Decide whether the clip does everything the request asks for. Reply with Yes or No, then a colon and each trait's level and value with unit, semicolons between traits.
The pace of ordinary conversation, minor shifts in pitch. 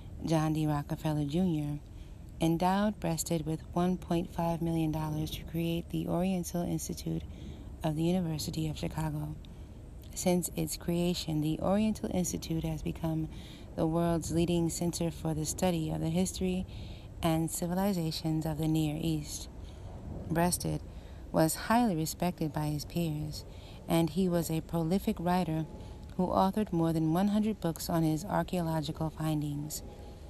No: slow, 130 wpm; narrow, 2.0 semitones